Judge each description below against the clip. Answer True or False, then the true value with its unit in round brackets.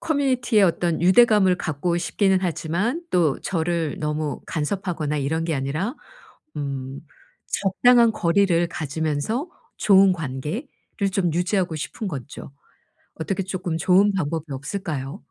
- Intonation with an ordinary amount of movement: True (4.5 semitones)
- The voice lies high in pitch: False (175 Hz)